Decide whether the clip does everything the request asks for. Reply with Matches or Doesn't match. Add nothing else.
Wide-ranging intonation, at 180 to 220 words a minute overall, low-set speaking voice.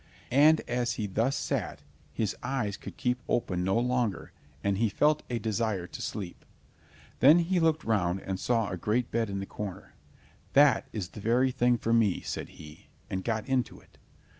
Doesn't match